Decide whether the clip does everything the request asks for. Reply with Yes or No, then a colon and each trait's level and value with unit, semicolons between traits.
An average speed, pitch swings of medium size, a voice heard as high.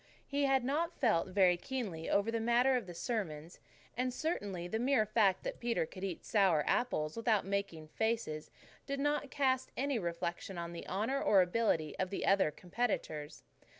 No: average, 175 wpm; wide, 6.2 semitones; high, 205 Hz